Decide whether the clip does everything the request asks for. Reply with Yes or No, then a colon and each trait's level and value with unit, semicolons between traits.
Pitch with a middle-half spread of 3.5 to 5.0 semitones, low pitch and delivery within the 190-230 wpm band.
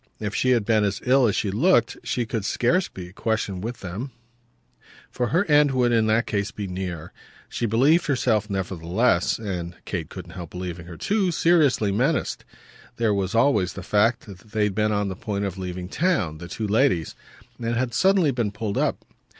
Yes: average, 4.7 semitones; low, 105 Hz; average, 195 wpm